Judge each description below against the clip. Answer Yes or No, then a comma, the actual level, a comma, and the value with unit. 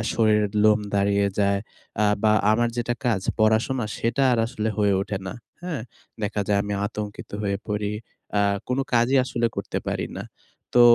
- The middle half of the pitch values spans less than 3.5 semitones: Yes, narrow, 2.5 semitones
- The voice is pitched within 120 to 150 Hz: No, low, 110 Hz